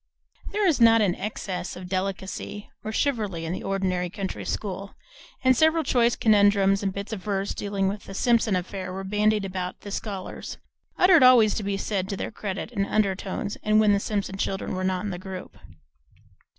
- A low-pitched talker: No, high, 200 Hz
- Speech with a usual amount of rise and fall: No, narrow, 2.1 semitones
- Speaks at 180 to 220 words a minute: Yes, average, 190 wpm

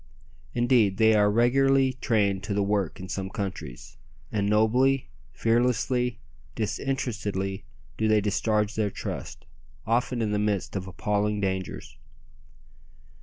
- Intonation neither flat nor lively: Yes, average, 3.1 semitones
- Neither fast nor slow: No, slow, 125 wpm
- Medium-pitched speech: No, low, 105 Hz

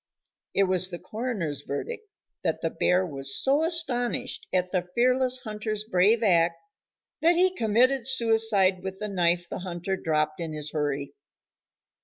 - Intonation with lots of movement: Yes, wide, 5.9 semitones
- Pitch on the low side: No, high, 195 Hz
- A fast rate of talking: No, average, 150 wpm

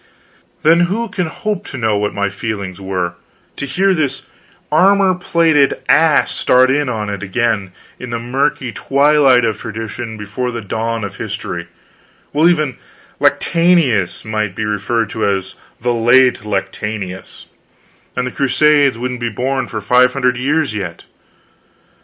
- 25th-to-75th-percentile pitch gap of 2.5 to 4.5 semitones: No, wide, 5.6 semitones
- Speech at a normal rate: Yes, average, 145 wpm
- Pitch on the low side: Yes, low, 125 Hz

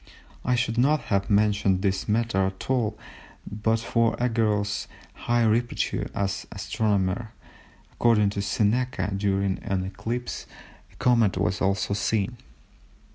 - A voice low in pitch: Yes, low, 105 Hz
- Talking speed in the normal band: No, slow, 130 wpm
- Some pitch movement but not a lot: Yes, average, 3.0 semitones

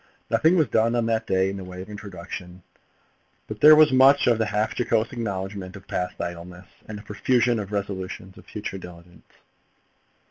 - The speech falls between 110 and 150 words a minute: No, average, 175 wpm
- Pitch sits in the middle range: No, low, 105 Hz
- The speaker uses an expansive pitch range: No, average, 3.7 semitones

